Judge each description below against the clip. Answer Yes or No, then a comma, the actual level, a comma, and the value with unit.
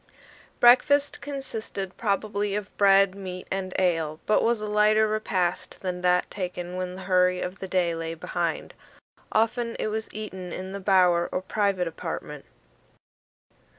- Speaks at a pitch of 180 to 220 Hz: Yes, high, 190 Hz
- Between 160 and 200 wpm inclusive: No, average, 150 wpm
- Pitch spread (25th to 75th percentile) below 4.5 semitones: Yes, average, 2.8 semitones